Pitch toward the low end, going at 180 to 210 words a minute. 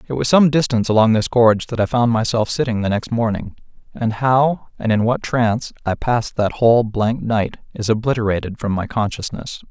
Yes: low, 115 Hz; average, 200 wpm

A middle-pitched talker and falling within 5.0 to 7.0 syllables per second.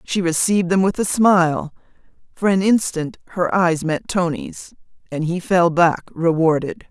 No: medium, 175 Hz; 4.5 syllables/s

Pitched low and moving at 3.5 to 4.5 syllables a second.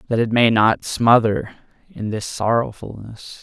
Yes: low, 110 Hz; 4.2 syllables/s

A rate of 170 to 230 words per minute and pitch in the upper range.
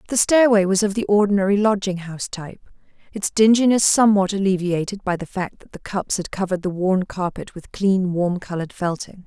Yes: average, 190 wpm; high, 195 Hz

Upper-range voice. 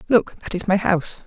Yes: high, 195 Hz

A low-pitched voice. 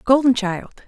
No: high, 235 Hz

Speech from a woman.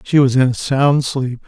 No: male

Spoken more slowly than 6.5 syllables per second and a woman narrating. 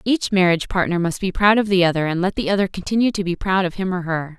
No: 6.6 syllables/s; female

